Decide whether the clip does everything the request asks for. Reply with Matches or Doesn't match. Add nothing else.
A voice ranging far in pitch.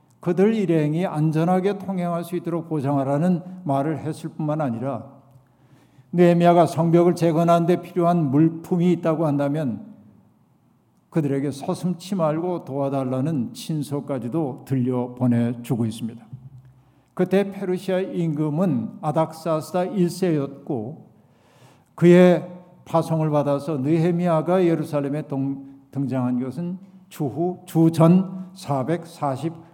Doesn't match